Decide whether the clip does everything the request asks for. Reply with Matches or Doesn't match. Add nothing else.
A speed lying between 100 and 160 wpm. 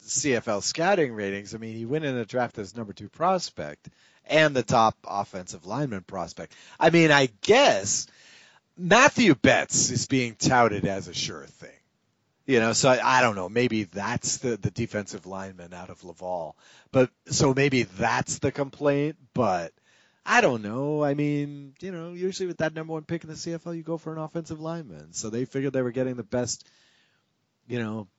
Doesn't match